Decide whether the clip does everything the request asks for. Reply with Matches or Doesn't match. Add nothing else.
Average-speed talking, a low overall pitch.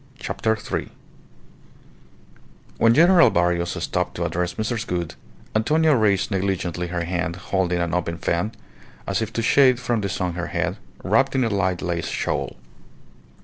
Matches